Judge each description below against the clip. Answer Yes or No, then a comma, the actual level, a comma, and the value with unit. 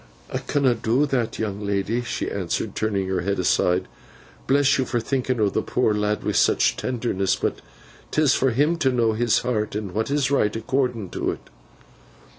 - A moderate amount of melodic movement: Yes, average, 3.9 semitones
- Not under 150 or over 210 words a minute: Yes, average, 185 wpm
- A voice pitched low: Yes, low, 115 Hz